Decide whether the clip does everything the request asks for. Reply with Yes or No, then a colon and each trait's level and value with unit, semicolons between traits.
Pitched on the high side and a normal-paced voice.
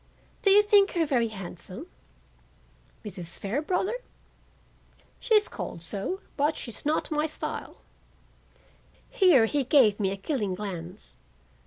No: very high, 260 Hz; slow, 120 wpm